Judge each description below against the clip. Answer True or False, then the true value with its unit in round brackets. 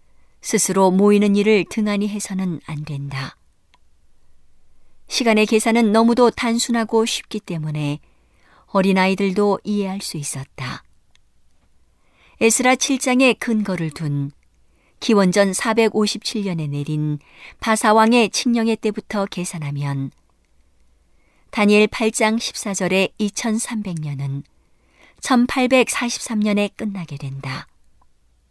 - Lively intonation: True (7.8 semitones)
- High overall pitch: True (195 Hz)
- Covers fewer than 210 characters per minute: True (195 characters per minute)